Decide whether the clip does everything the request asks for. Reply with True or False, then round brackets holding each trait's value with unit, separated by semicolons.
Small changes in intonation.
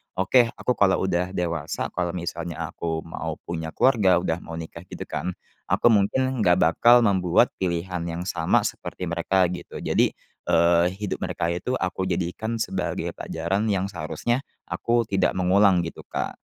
False (3.0 semitones)